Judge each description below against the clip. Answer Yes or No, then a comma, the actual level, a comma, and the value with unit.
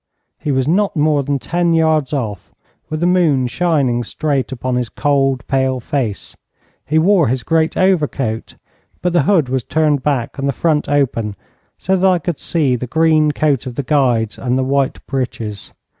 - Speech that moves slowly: No, average, 180 wpm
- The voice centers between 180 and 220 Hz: No, medium, 140 Hz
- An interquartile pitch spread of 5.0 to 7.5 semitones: No, average, 3.7 semitones